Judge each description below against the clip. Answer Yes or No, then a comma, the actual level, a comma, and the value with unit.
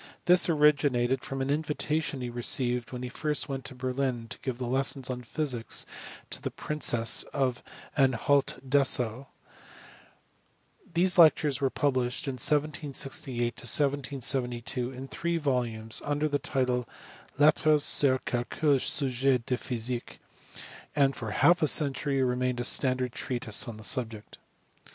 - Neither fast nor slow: No, slow, 130 wpm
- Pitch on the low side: Yes, low, 130 Hz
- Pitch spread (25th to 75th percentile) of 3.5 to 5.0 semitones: No, average, 2.8 semitones